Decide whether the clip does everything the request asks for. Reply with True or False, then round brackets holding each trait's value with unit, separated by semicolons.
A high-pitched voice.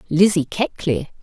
False (180 Hz)